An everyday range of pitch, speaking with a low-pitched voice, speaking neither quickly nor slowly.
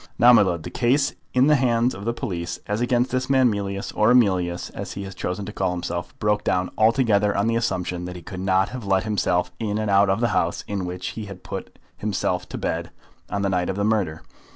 No: average, 3.9 semitones; low, 100 Hz; fast, 240 wpm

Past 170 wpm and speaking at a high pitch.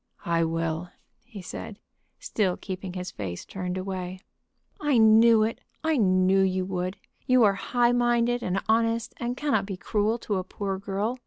No: average, 165 wpm; high, 200 Hz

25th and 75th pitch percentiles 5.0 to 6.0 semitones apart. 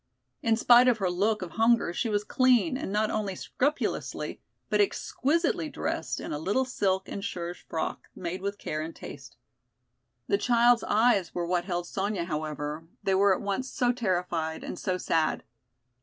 Yes: wide, 5.4 semitones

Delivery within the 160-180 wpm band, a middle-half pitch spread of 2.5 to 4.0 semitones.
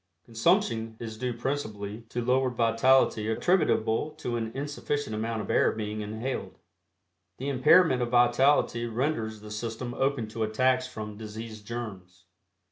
No: slow, 135 wpm; average, 2.8 semitones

